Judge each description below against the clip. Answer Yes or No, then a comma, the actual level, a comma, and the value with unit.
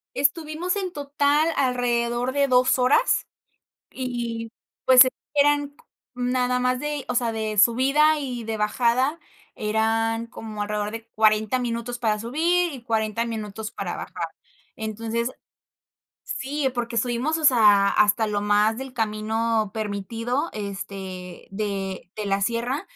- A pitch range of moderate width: Yes, average, 3.5 semitones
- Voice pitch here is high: Yes, high, 235 Hz